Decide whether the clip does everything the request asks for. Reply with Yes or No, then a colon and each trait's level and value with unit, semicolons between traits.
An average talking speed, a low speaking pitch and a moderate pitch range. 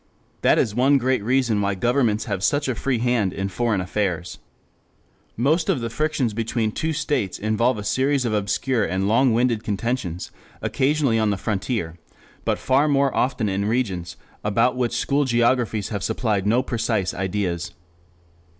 Yes: average, 160 wpm; low, 115 Hz; average, 4.2 semitones